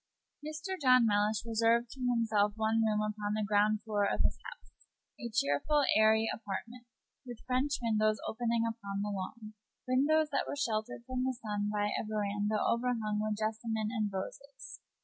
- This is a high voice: Yes, high, 220 Hz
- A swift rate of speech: No, average, 165 wpm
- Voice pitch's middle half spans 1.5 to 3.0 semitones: Yes, average, 2.7 semitones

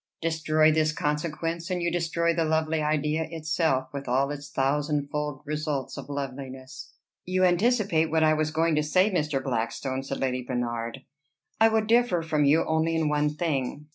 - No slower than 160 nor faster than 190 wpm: Yes, average, 170 wpm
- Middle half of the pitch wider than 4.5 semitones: No, average, 2.8 semitones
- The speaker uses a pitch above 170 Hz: No, medium, 155 Hz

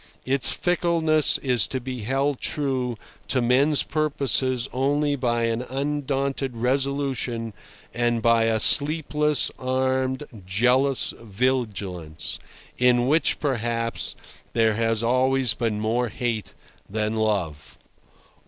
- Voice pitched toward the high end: No, low, 125 Hz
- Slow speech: Yes, slow, 105 wpm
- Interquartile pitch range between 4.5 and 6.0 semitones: No, average, 3.2 semitones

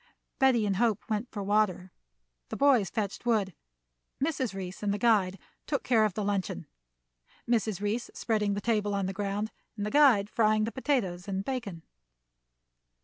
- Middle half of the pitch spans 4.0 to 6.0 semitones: No, average, 2.9 semitones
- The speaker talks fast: No, average, 165 wpm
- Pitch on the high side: Yes, high, 210 Hz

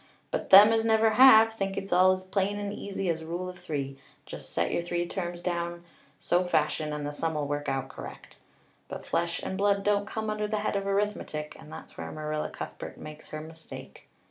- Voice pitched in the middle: Yes, medium, 180 Hz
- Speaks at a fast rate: Yes, fast, 210 wpm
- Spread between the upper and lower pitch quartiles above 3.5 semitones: Yes, average, 4.7 semitones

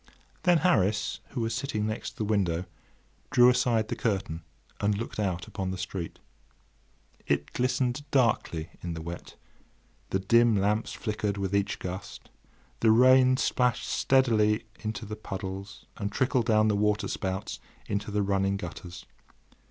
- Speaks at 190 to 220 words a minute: No, average, 145 wpm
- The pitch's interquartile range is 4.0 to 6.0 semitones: No, average, 3.4 semitones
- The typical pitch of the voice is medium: No, low, 105 Hz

